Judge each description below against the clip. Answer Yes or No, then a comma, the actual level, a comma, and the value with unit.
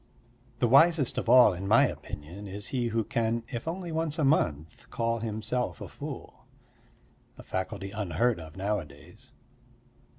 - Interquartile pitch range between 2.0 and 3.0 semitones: No, average, 4.7 semitones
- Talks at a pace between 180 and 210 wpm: No, average, 145 wpm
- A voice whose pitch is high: No, low, 115 Hz